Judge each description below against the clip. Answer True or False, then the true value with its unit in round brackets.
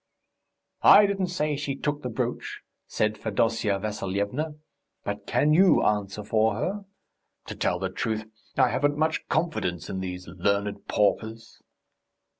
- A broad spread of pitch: True (6.7 semitones)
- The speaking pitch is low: True (110 Hz)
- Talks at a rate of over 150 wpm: False (135 wpm)